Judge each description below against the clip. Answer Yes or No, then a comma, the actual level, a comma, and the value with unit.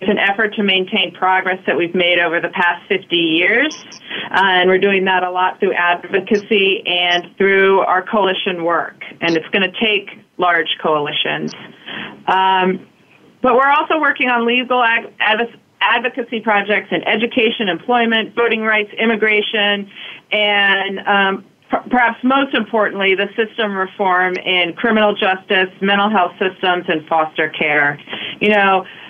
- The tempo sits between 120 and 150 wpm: Yes, average, 145 wpm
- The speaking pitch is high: Yes, high, 195 Hz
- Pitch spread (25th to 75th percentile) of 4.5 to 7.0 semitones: No, average, 3.4 semitones